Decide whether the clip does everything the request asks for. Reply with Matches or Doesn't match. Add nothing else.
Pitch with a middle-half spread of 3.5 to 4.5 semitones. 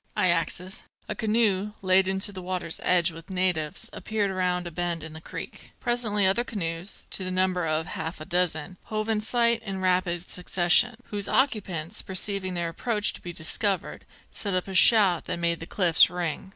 Doesn't match